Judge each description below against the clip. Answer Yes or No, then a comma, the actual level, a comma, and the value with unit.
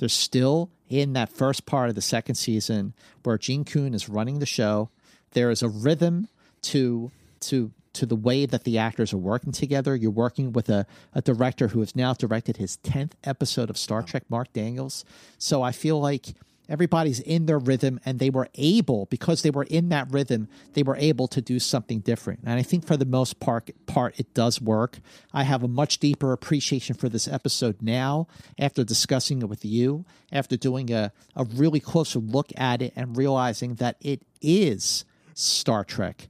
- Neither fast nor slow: Yes, average, 195 wpm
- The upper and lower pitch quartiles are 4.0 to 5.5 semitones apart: No, average, 3.3 semitones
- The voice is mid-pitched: No, low, 130 Hz